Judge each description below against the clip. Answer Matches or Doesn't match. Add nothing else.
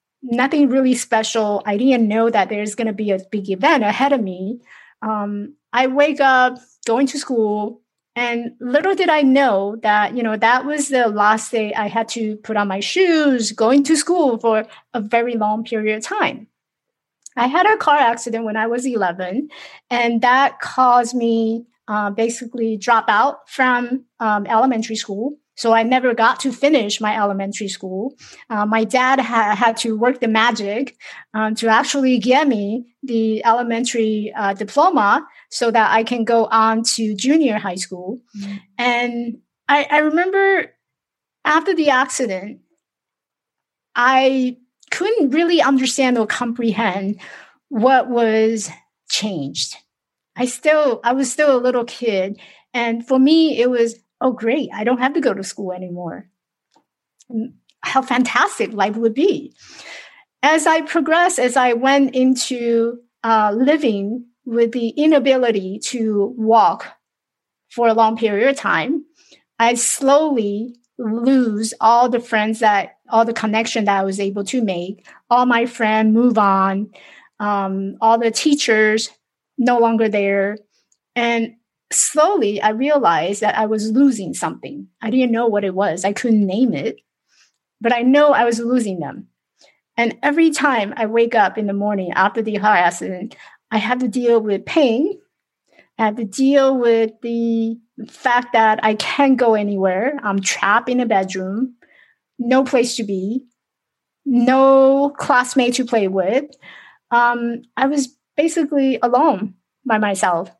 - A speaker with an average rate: Matches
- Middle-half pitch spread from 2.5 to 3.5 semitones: Matches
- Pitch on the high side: Matches